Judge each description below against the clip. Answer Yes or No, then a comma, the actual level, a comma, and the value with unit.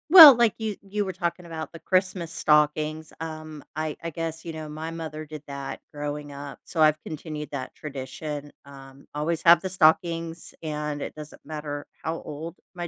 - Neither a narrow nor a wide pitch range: No, narrow, 2.1 semitones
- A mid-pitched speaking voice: Yes, medium, 155 Hz